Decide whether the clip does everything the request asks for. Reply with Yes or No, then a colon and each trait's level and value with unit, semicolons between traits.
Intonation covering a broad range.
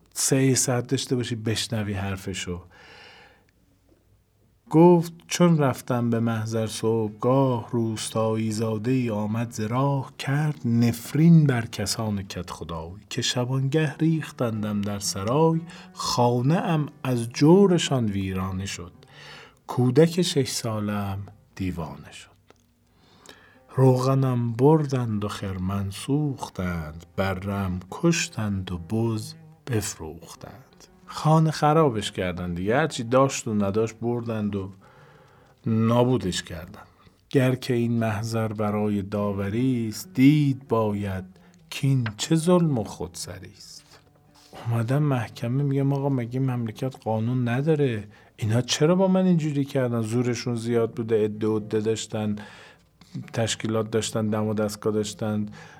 No: average, 4.5 semitones